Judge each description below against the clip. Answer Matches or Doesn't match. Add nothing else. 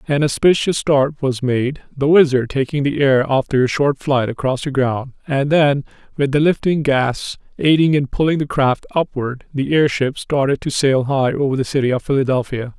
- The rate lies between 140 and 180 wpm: Doesn't match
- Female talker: Doesn't match